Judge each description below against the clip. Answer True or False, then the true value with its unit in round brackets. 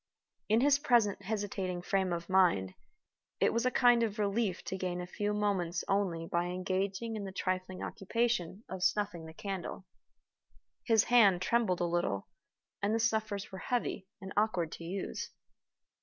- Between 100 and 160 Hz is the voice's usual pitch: False (195 Hz)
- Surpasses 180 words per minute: False (160 wpm)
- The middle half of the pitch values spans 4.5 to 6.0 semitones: False (3.3 semitones)